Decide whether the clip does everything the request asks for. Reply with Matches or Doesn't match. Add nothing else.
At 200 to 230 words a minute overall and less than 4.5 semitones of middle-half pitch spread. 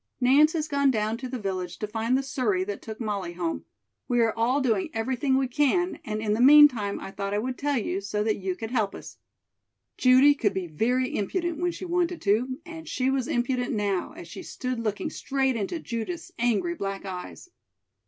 Doesn't match